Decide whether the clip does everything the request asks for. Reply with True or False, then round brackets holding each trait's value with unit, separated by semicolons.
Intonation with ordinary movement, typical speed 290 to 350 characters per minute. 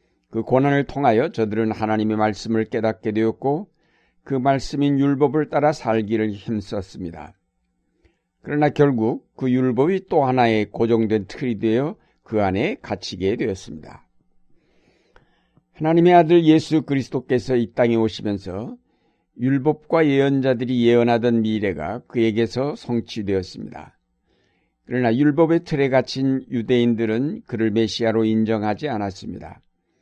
True (4.2 semitones; 295 characters per minute)